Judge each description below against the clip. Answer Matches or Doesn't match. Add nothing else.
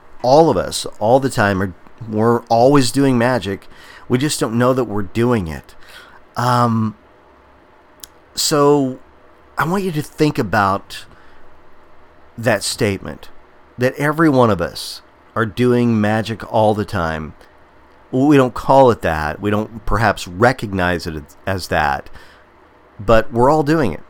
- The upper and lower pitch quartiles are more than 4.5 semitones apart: Matches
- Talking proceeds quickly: Doesn't match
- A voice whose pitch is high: Doesn't match